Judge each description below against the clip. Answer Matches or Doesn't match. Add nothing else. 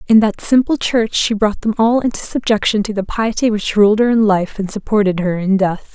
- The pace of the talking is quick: Matches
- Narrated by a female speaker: Matches